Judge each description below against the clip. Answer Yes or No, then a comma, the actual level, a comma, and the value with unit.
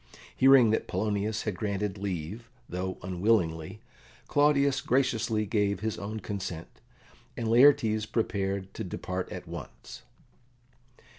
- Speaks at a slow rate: Yes, slow, 115 wpm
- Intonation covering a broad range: No, average, 3.3 semitones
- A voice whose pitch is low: Yes, low, 105 Hz